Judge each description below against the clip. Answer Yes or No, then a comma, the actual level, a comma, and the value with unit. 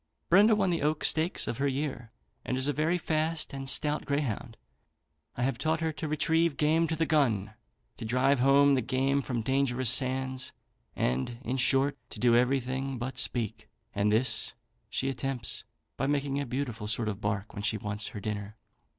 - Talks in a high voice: No, low, 135 Hz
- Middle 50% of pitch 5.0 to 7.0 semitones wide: No, average, 3.8 semitones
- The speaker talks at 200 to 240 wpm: No, average, 185 wpm